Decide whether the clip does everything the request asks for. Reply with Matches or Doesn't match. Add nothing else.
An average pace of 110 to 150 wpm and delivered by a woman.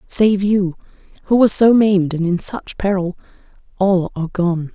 Matches